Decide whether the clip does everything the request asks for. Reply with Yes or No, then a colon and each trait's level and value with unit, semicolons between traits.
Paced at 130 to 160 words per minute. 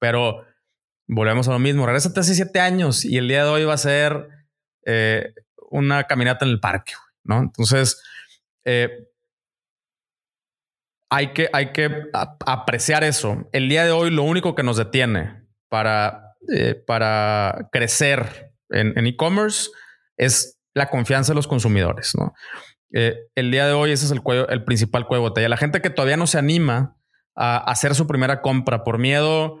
No: average, 170 wpm